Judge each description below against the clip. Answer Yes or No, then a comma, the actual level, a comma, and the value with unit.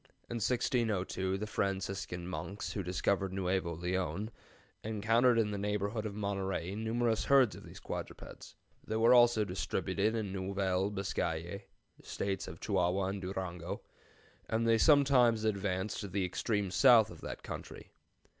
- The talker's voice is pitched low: Yes, low, 100 Hz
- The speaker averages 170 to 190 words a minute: No, average, 140 wpm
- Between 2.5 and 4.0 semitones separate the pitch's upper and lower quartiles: Yes, average, 2.9 semitones